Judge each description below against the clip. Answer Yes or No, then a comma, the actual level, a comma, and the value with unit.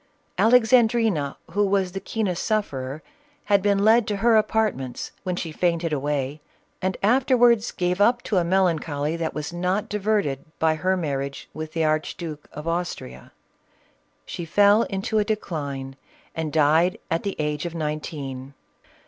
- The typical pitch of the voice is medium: Yes, medium, 175 Hz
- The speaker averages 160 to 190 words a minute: No, average, 150 wpm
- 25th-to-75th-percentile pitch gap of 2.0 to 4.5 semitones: No, average, 5.3 semitones